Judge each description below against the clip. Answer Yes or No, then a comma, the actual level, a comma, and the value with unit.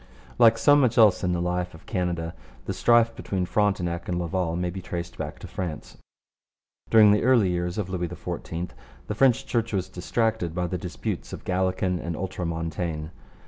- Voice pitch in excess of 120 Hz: No, very low, 90 Hz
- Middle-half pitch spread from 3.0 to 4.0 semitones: Yes, average, 3.3 semitones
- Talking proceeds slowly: No, average, 180 wpm